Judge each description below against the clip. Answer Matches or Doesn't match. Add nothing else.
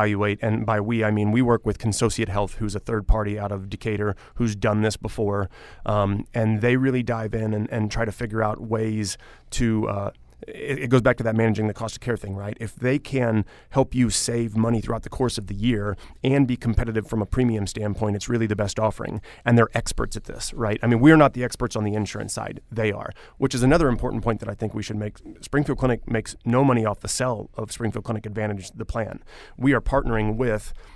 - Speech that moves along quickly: Matches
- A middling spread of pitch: Doesn't match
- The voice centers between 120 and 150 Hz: Doesn't match